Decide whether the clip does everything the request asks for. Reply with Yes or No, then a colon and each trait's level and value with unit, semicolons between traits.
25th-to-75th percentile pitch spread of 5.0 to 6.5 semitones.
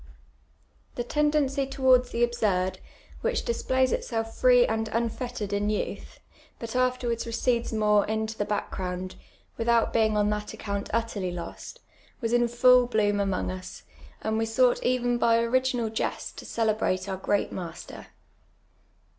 No: average, 3.0 semitones